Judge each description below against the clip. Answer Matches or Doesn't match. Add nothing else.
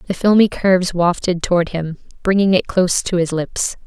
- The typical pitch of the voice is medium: Matches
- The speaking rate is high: Doesn't match